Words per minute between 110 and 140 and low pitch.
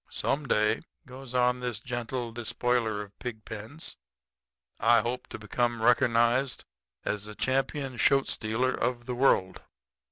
Yes: slow, 135 wpm; low, 120 Hz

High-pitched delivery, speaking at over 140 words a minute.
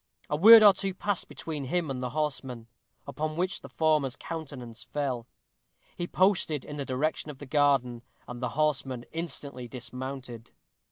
No: medium, 145 Hz; average, 160 wpm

